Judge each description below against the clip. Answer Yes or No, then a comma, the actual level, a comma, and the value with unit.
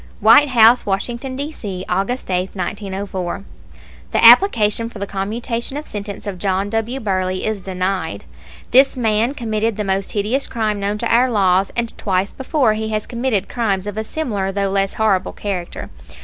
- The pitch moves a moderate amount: Yes, average, 3.3 semitones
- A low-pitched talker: No, high, 210 Hz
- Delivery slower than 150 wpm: No, average, 170 wpm